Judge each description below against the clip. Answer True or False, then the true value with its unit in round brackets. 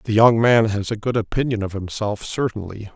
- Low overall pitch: True (110 Hz)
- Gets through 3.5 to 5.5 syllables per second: True (5.4 syllables/s)